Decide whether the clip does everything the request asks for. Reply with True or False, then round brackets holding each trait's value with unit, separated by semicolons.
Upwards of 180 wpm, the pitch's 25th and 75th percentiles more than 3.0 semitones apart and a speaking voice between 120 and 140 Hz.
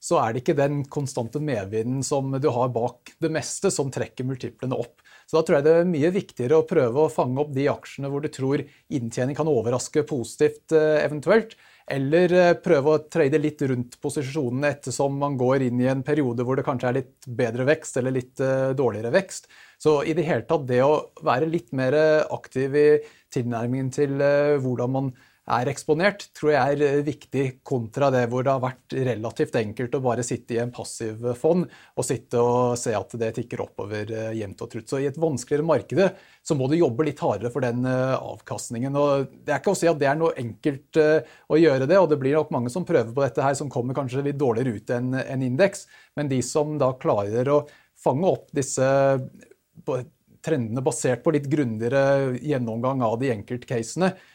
True (195 wpm; 3.5 semitones; 135 Hz)